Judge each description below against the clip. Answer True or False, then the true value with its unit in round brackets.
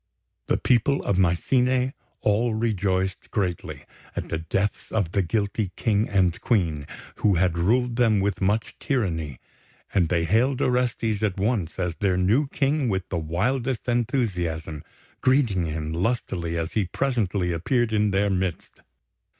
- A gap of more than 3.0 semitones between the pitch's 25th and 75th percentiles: True (5.1 semitones)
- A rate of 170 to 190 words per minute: False (145 wpm)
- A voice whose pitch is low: True (100 Hz)